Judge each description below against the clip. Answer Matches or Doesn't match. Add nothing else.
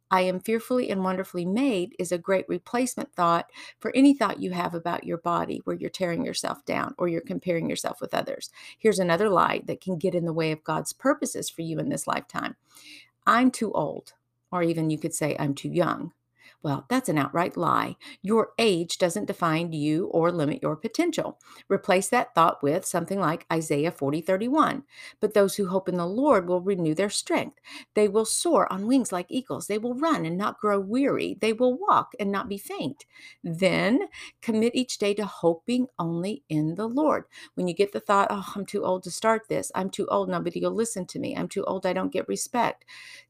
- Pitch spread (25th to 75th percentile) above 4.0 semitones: Matches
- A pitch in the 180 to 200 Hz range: Matches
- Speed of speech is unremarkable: Doesn't match